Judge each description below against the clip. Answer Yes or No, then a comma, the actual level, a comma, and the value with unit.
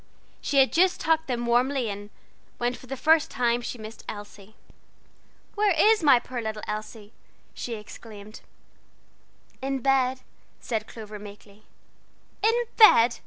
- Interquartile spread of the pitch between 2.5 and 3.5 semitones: No, average, 4.0 semitones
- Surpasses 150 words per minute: No, slow, 135 wpm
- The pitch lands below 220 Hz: No, high, 240 Hz